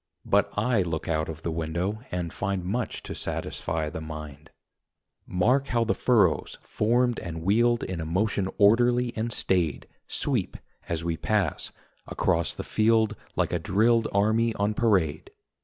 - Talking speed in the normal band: Yes, average, 155 wpm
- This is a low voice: Yes, low, 100 Hz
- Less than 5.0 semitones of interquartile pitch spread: No, wide, 5.5 semitones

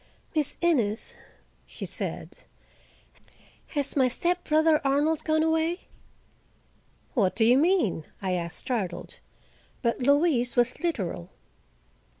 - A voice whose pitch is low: No, very high, 280 Hz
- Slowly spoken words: Yes, slow, 105 wpm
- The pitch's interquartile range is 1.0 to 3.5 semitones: No, wide, 5.5 semitones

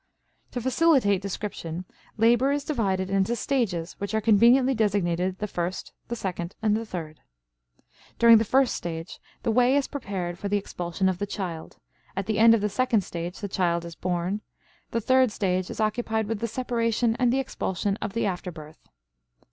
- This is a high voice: Yes, high, 205 Hz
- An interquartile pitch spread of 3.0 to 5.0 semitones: Yes, average, 4.3 semitones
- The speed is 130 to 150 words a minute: No, average, 180 wpm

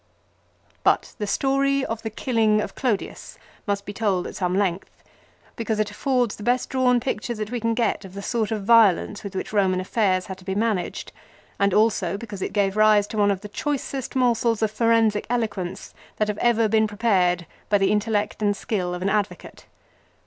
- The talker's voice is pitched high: Yes, high, 210 Hz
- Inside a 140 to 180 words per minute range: No, average, 195 wpm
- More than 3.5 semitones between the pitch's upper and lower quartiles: No, narrow, 2.5 semitones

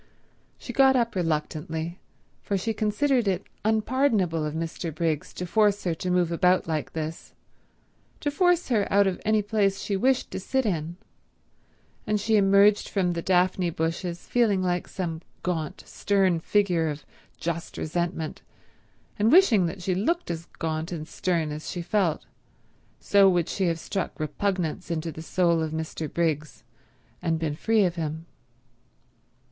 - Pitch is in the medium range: Yes, medium, 180 Hz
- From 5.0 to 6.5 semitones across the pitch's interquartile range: No, average, 4.0 semitones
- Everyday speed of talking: Yes, average, 155 wpm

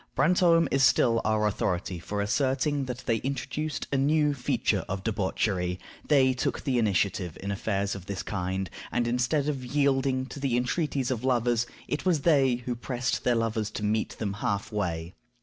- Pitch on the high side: No, low, 120 Hz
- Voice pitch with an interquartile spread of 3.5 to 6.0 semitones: Yes, average, 4.9 semitones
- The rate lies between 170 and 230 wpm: Yes, average, 175 wpm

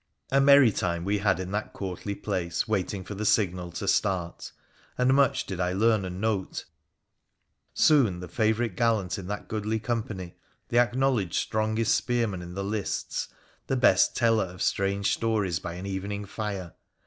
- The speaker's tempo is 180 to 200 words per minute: No, average, 170 wpm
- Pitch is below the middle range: Yes, low, 100 Hz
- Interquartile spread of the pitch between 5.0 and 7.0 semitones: No, average, 3.3 semitones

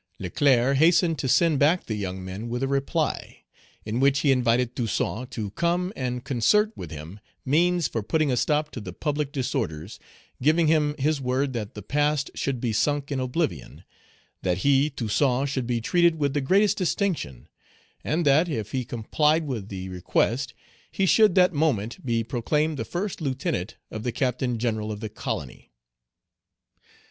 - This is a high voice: No, low, 135 Hz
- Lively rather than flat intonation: No, average, 5.0 semitones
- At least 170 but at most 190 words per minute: Yes, average, 175 wpm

